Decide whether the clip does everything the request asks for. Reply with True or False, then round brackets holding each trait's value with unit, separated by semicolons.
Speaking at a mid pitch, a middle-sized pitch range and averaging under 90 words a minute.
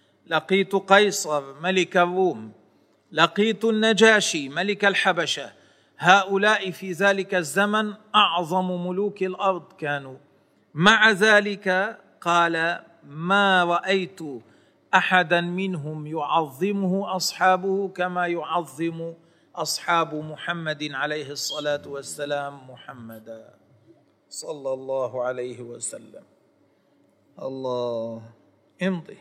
True (175 Hz; 4.7 semitones; 80 wpm)